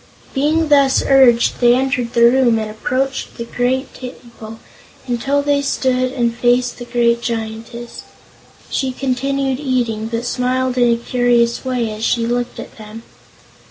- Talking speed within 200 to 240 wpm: No, average, 150 wpm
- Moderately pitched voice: No, high, 245 Hz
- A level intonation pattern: Yes, narrow, 1.9 semitones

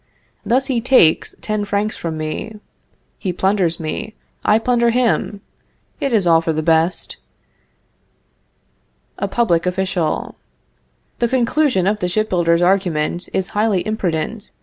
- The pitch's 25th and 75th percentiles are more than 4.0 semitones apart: Yes, average, 4.8 semitones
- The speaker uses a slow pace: Yes, slow, 130 wpm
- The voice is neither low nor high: No, high, 195 Hz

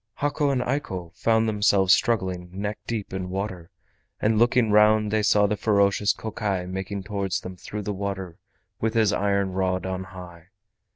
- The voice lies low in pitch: Yes, low, 100 Hz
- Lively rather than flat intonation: No, narrow, 2.5 semitones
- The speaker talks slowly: No, average, 165 wpm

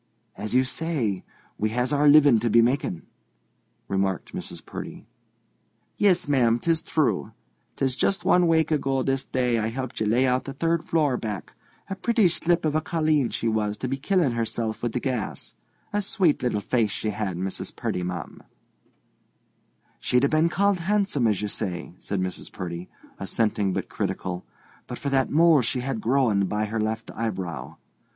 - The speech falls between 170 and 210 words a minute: Yes, average, 175 wpm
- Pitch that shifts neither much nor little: No, wide, 6.2 semitones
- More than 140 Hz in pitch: No, low, 125 Hz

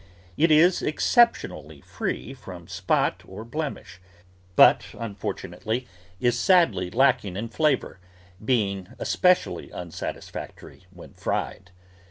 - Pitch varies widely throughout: Yes, wide, 8.0 semitones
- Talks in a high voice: No, low, 115 Hz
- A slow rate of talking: Yes, slow, 105 wpm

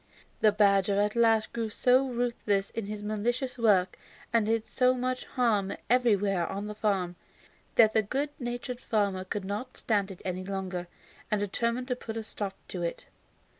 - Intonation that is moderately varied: Yes, average, 3.4 semitones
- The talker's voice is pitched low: No, high, 215 Hz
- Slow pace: No, average, 170 wpm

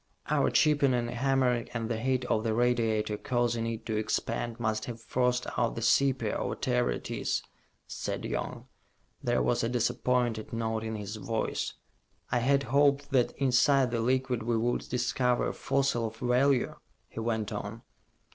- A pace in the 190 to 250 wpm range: No, average, 165 wpm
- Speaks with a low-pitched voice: Yes, low, 120 Hz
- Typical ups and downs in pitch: No, narrow, 2.2 semitones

